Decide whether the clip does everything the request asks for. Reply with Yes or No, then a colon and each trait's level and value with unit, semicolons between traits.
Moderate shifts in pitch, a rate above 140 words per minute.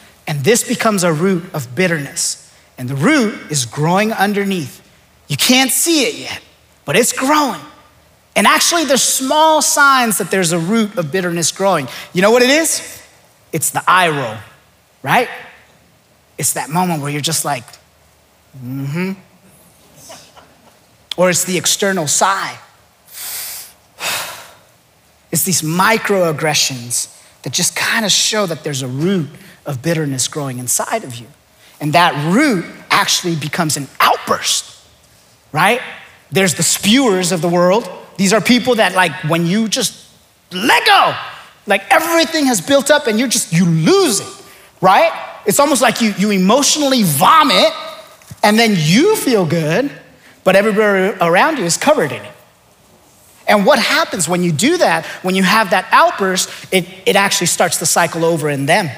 No: wide, 6.0 semitones; average, 155 wpm